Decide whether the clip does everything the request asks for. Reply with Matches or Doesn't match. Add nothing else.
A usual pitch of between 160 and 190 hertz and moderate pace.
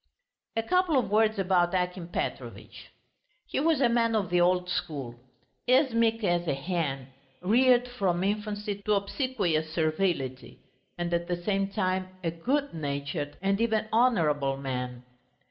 Matches